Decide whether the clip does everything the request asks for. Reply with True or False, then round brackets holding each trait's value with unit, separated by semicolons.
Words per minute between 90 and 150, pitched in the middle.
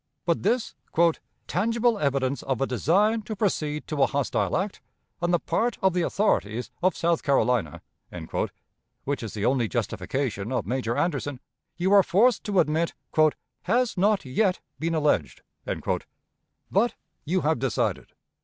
True (145 wpm; 160 Hz)